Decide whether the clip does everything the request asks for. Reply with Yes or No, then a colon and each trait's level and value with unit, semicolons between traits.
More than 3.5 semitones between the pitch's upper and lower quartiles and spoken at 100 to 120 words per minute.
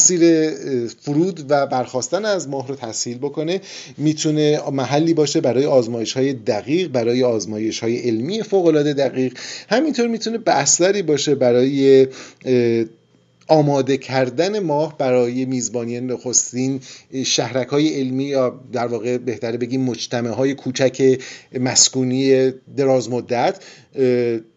No: average, 3.1 semitones; average, 115 wpm